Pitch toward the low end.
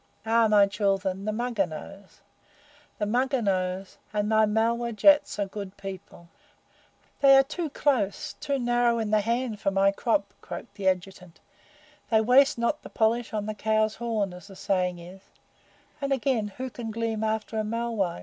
No: high, 215 Hz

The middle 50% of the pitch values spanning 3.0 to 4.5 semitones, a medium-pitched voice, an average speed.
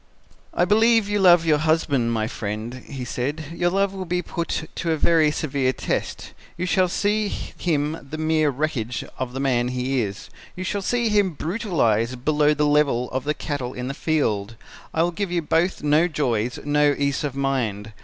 No: average, 5.3 semitones; medium, 150 Hz; average, 190 wpm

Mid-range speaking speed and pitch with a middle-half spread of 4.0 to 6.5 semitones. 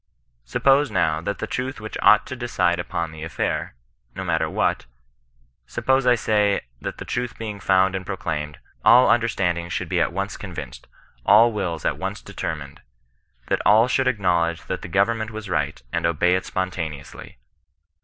Yes: average, 175 wpm; average, 5.1 semitones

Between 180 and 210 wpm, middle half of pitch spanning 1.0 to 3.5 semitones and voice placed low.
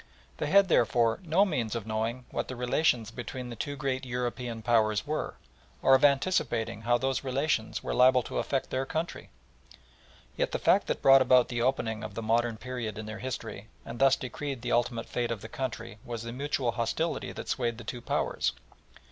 Yes: average, 195 wpm; narrow, 2.6 semitones; low, 120 Hz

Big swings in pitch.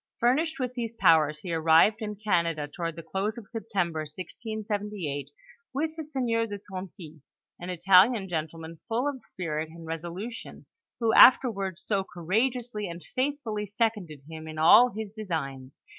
Yes: wide, 5.7 semitones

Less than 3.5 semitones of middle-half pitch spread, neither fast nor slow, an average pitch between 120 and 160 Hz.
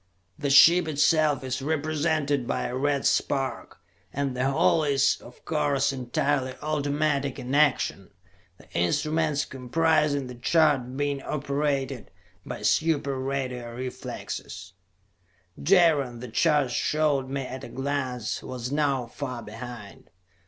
No: average, 2.8 semitones; slow, 125 wpm; medium, 140 Hz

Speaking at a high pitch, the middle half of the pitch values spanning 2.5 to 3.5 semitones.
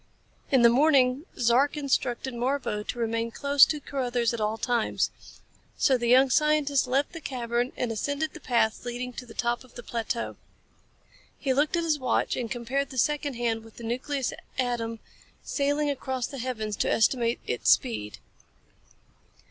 Yes: very high, 250 Hz; average, 3.0 semitones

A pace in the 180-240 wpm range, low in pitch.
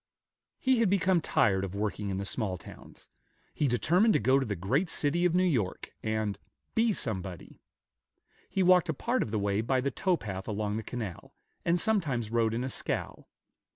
Yes: average, 190 wpm; low, 120 Hz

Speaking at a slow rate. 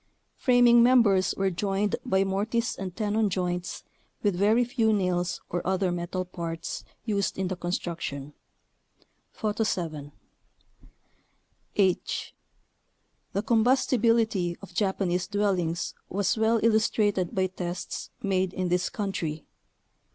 Yes: slow, 115 wpm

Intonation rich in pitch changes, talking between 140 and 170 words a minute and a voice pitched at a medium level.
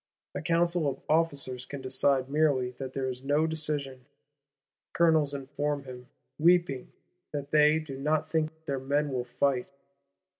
No: average, 2.8 semitones; average, 145 wpm; medium, 145 Hz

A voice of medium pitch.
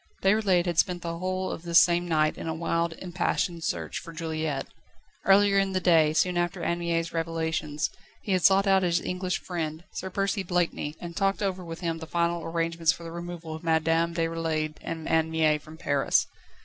Yes: medium, 170 Hz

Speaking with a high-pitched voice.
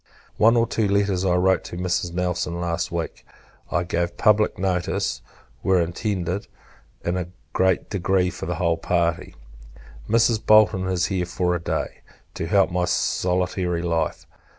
No: very low, 90 Hz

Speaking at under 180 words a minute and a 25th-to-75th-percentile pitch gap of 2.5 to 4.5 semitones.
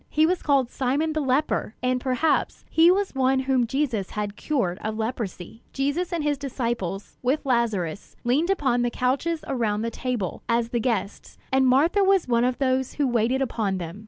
No: average, 185 wpm; average, 3.8 semitones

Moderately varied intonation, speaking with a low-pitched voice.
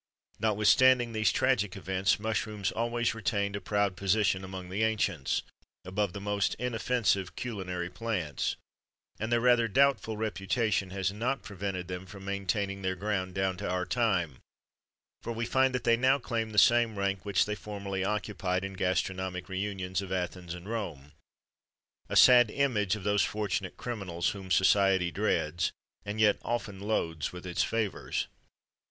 Yes: average, 3.1 semitones; low, 100 Hz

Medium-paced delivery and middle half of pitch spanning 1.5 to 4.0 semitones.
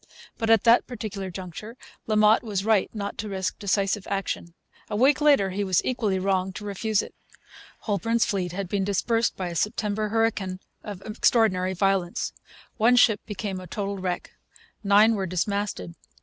Yes: average, 165 wpm; narrow, 2.6 semitones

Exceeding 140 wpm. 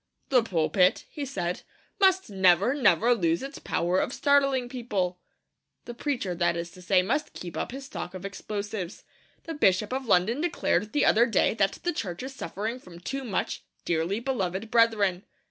Yes: average, 175 wpm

